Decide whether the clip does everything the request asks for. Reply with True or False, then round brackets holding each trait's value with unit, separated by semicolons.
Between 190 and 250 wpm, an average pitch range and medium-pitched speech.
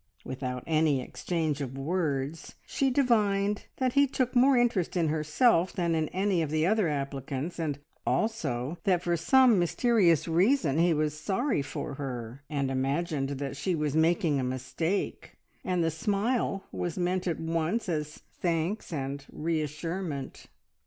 False (150 wpm; 5.0 semitones; 165 Hz)